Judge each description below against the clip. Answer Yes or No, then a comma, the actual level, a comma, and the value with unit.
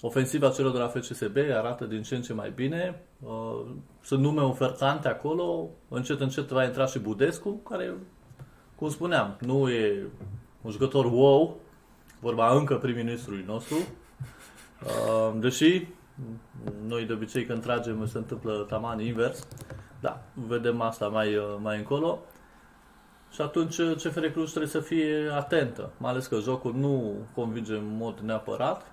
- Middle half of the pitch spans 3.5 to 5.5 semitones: Yes, average, 3.8 semitones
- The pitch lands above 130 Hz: No, low, 125 Hz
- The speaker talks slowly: No, average, 140 wpm